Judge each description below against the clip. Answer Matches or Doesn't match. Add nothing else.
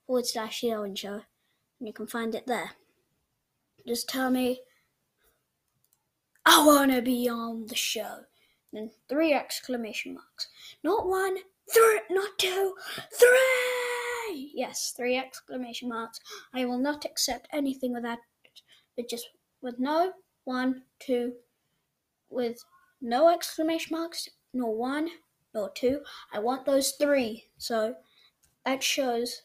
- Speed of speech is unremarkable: Doesn't match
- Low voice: Doesn't match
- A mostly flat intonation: Doesn't match